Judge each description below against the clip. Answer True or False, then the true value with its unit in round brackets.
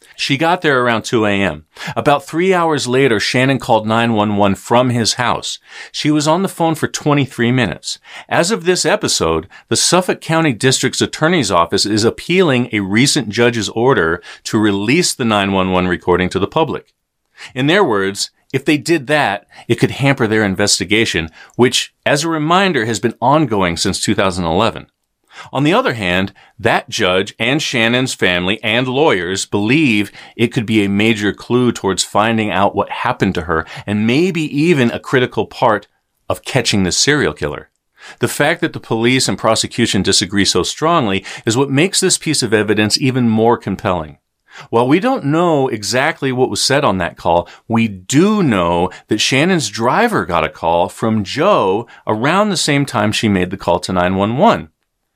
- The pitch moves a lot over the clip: True (6.2 semitones)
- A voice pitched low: True (115 Hz)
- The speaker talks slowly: False (170 wpm)